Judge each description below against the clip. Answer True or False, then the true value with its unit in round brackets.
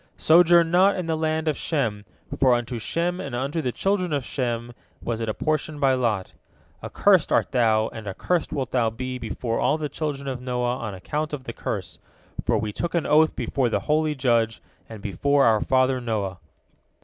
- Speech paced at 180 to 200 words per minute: True (190 wpm)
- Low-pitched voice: True (130 Hz)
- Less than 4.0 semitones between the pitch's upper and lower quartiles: False (5.2 semitones)